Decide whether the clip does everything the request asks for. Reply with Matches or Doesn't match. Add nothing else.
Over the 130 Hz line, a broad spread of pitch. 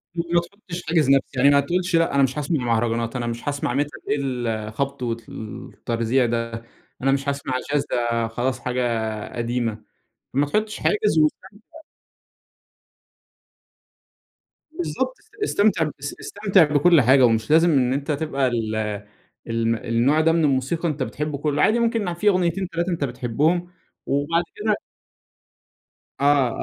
Matches